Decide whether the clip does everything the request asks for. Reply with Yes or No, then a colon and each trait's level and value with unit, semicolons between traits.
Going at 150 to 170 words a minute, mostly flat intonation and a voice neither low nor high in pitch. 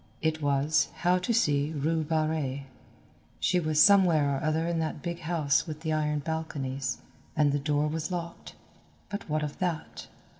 Yes: average, 165 wpm; narrow, 2.2 semitones; medium, 155 Hz